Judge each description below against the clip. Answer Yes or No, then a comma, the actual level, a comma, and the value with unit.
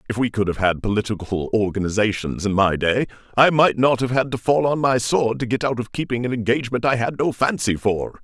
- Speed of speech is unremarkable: No, fast, 235 wpm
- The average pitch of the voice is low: Yes, low, 115 Hz